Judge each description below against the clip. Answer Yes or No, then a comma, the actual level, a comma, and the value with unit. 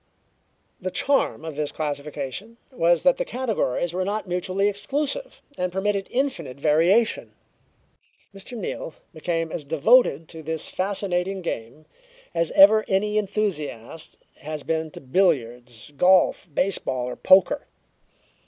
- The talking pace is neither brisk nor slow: No, slow, 125 wpm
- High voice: No, medium, 180 Hz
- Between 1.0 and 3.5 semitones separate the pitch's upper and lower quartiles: No, average, 4.9 semitones